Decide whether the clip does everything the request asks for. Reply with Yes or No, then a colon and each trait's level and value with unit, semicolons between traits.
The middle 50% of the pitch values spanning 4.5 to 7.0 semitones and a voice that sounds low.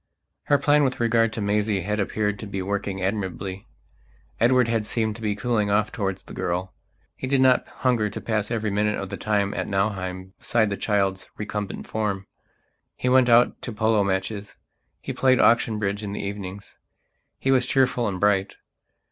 No: average, 2.7 semitones; low, 105 Hz